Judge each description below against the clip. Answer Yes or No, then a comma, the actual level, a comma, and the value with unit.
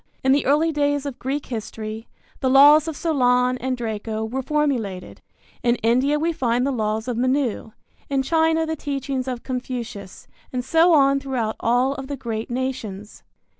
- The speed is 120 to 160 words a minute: No, average, 170 wpm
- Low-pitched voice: No, very high, 260 Hz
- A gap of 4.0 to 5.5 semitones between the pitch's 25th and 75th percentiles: No, average, 3.4 semitones